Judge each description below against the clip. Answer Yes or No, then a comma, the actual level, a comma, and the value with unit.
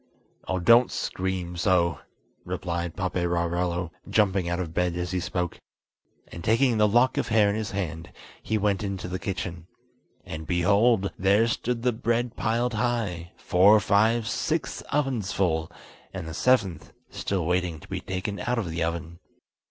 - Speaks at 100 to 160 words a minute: Yes, average, 155 wpm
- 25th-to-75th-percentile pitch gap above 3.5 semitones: Yes, average, 4.1 semitones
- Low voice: Yes, very low, 95 Hz